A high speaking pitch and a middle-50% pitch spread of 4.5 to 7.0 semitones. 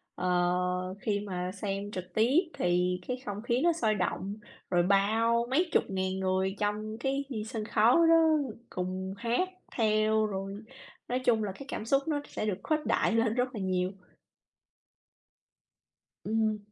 No: high, 215 Hz; average, 3.8 semitones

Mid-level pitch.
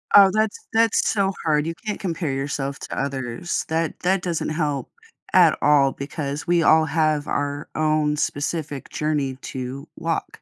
Yes: medium, 155 Hz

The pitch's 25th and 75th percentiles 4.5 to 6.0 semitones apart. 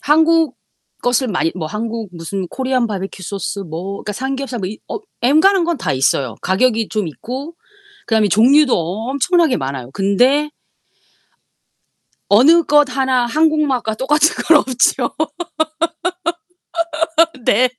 No: wide, 6.7 semitones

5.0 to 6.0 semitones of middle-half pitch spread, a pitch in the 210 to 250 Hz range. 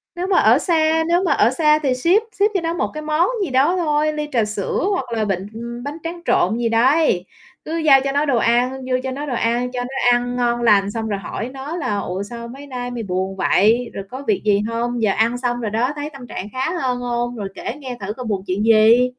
No: average, 4.6 semitones; high, 245 Hz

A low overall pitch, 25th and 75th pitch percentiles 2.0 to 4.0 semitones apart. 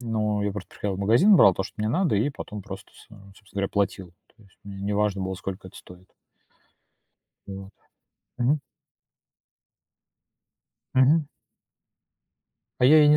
No: low, 105 Hz; average, 4.4 semitones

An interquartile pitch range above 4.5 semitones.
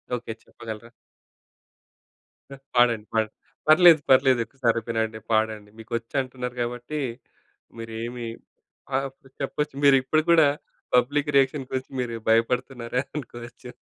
No: average, 2.7 semitones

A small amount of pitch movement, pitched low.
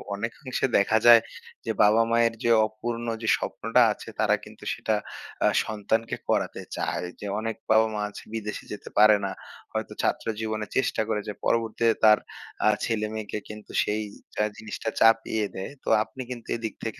Yes: narrow, 1.3 semitones; low, 110 Hz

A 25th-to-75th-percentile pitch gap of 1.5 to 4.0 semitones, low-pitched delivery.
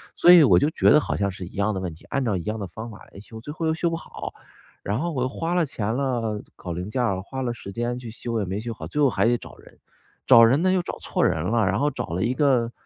No: average, 5.3 semitones; low, 115 Hz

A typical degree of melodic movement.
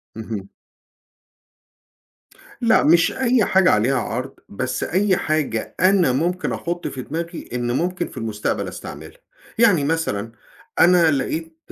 No: wide, 6.3 semitones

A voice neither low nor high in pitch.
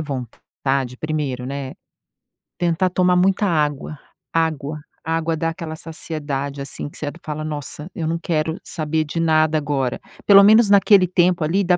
Yes: medium, 155 Hz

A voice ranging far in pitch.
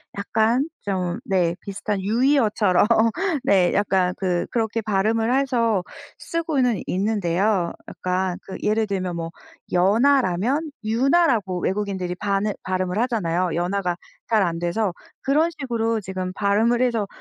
No: average, 3.8 semitones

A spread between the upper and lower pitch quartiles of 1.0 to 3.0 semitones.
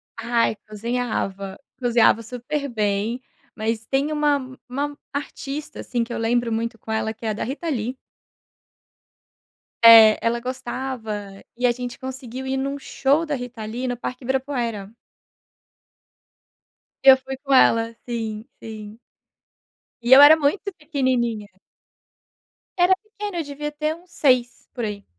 No: average, 3.6 semitones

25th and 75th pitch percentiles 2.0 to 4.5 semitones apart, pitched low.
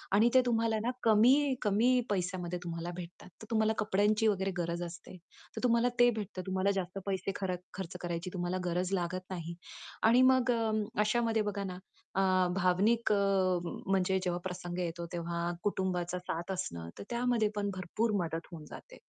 No: average, 3.7 semitones; high, 190 Hz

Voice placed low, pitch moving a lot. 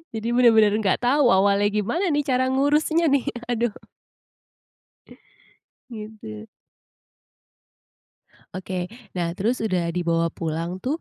No: high, 215 Hz; wide, 5.9 semitones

